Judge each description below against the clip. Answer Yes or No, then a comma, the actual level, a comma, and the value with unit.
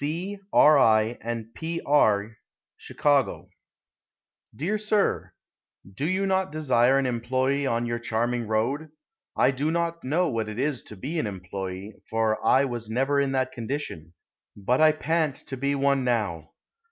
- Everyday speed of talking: Yes, average, 155 wpm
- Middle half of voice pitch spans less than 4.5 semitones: No, average, 5.1 semitones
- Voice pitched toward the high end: No, low, 130 Hz